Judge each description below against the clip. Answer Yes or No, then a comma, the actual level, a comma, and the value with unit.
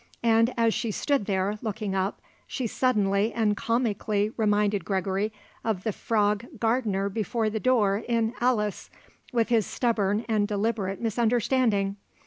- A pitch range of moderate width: No, narrow, 2.3 semitones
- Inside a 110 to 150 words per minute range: Yes, slow, 135 wpm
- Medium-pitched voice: No, high, 215 Hz